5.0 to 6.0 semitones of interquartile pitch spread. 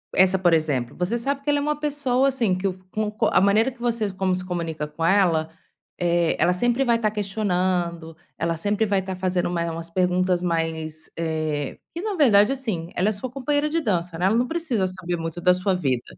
Yes: wide, 5.5 semitones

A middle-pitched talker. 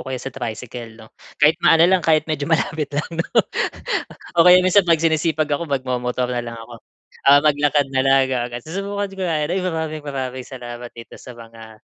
Yes: medium, 145 Hz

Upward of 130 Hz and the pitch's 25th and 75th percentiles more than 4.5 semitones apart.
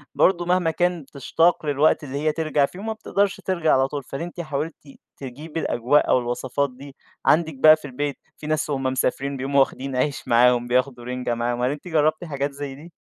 No: medium, 140 Hz; average, 3.2 semitones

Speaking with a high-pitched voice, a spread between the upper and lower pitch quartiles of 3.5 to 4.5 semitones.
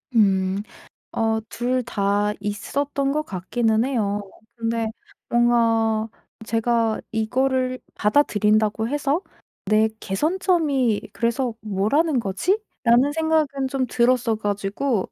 Yes: high, 230 Hz; average, 4.1 semitones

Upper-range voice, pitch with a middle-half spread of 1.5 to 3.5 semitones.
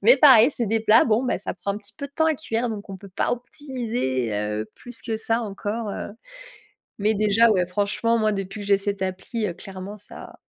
Yes: high, 215 Hz; average, 2.9 semitones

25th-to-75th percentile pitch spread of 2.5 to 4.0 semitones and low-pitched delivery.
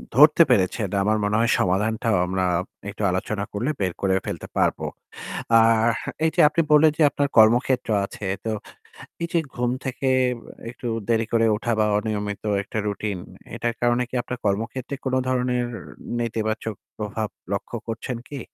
Yes: average, 3.1 semitones; low, 115 Hz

